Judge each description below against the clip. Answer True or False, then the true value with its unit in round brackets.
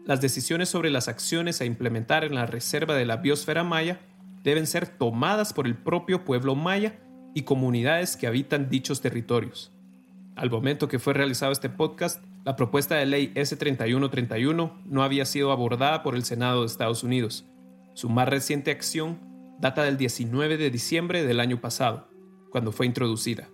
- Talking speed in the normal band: True (165 wpm)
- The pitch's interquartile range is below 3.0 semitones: False (4.7 semitones)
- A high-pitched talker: False (140 Hz)